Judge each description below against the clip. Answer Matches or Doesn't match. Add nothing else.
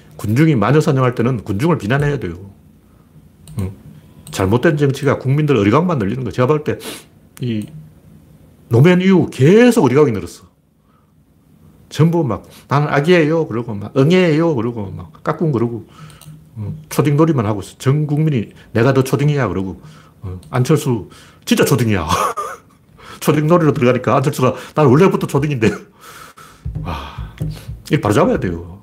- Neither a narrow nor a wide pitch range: Doesn't match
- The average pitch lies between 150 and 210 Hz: Doesn't match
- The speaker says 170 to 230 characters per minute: Doesn't match